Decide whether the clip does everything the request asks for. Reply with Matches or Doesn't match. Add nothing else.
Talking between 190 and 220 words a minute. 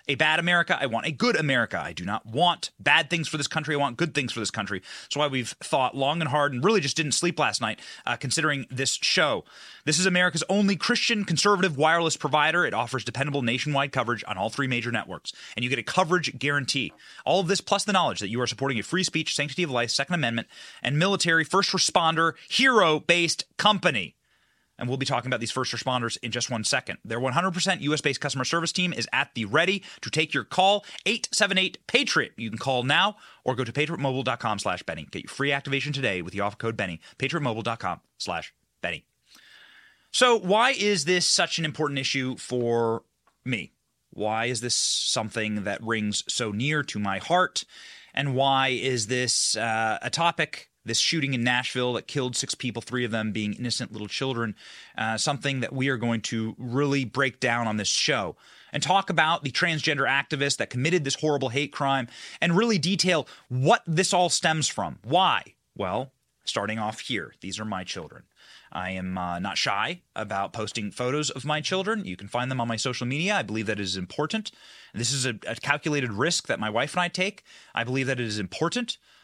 Matches